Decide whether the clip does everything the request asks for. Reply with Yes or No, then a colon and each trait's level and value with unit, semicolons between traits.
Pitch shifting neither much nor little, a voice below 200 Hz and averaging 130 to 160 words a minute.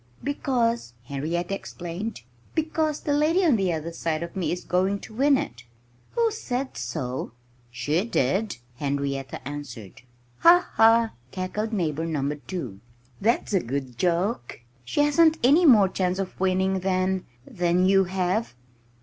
No: wide, 7.1 semitones; medium, 185 Hz; average, 145 wpm